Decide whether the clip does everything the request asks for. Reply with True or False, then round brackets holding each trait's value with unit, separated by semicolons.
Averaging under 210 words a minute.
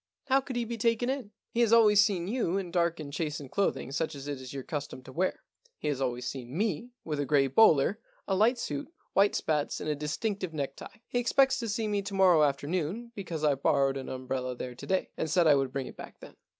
False (255 wpm)